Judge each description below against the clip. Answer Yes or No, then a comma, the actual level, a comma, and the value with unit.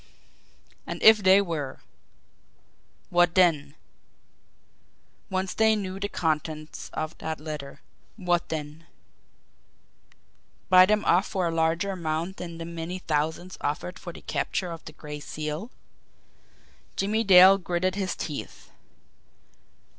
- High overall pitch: No, medium, 175 Hz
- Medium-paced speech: No, slow, 120 wpm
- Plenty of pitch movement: No, average, 3.2 semitones